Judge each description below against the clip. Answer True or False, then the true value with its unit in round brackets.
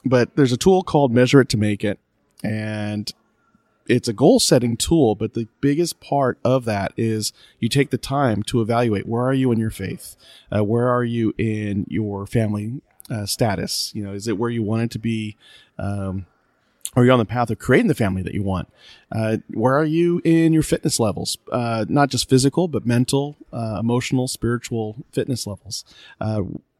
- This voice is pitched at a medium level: False (115 Hz)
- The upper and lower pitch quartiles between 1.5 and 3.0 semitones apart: False (3.6 semitones)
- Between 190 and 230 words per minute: True (195 wpm)